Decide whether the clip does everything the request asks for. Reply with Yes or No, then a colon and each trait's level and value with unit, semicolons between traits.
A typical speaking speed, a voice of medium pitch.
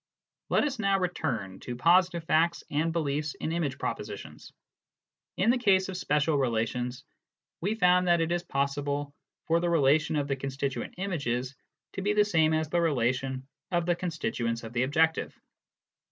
Yes: average, 165 wpm; medium, 155 Hz